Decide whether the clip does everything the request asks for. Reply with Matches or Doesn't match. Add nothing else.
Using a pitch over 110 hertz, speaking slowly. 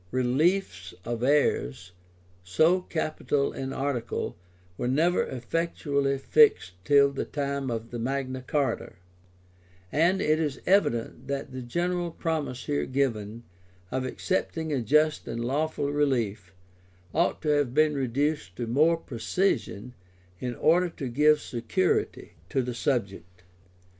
Matches